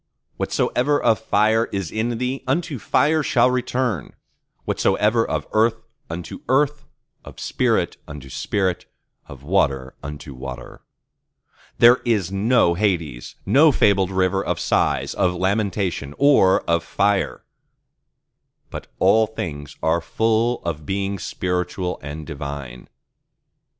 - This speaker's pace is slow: Yes, slow, 120 wpm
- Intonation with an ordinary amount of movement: No, wide, 6.0 semitones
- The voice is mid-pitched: No, very low, 95 Hz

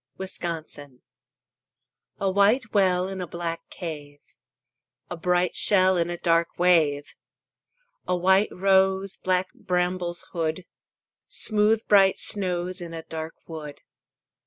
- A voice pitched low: No, medium, 180 Hz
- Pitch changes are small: Yes, narrow, 2.3 semitones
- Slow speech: Yes, slow, 115 wpm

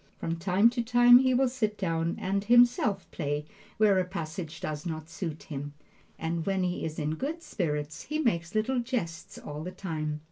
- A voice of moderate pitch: Yes, medium, 180 Hz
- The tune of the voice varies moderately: No, wide, 6.8 semitones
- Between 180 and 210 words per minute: Yes, average, 185 wpm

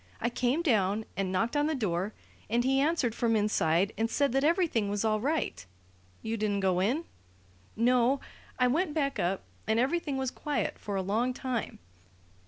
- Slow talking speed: No, average, 185 wpm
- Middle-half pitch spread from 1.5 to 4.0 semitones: No, average, 5.0 semitones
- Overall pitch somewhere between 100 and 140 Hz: No, high, 235 Hz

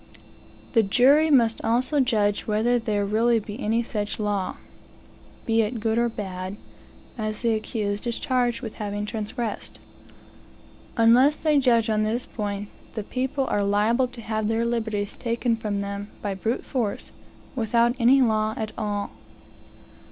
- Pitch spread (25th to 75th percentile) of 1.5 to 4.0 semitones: Yes, narrow, 2.4 semitones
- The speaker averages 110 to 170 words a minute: Yes, average, 150 wpm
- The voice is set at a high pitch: Yes, high, 225 Hz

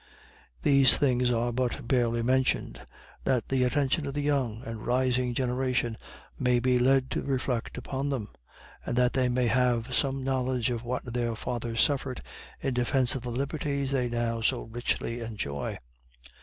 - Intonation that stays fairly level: Yes, narrow, 1.8 semitones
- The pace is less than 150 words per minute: No, average, 160 wpm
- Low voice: Yes, low, 125 Hz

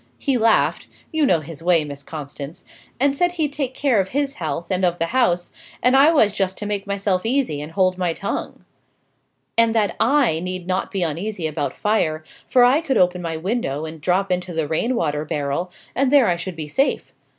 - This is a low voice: No, medium, 185 Hz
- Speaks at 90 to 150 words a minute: No, fast, 205 wpm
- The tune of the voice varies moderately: No, wide, 7.0 semitones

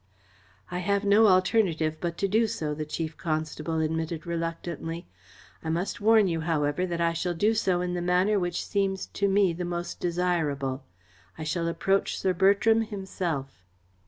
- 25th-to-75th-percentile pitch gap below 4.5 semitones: Yes, average, 3.1 semitones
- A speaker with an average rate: Yes, average, 165 wpm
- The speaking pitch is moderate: Yes, medium, 175 Hz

